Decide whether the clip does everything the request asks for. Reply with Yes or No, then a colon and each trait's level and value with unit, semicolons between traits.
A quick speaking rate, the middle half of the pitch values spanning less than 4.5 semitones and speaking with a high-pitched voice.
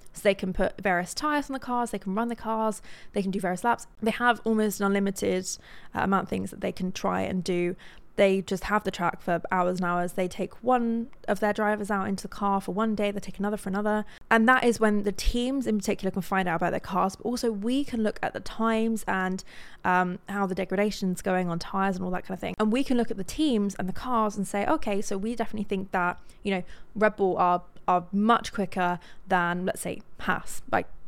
Yes: fast, 245 wpm; average, 3.0 semitones; high, 200 Hz